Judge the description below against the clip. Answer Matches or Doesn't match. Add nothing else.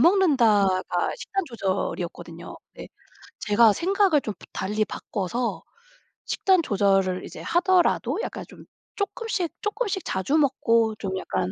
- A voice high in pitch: Matches